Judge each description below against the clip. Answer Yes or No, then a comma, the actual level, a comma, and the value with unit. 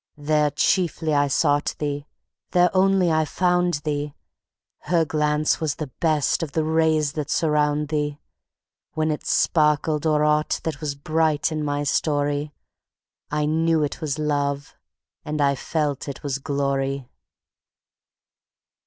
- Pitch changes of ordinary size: No, narrow, 1.6 semitones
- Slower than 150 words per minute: Yes, slow, 135 wpm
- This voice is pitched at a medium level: Yes, medium, 150 Hz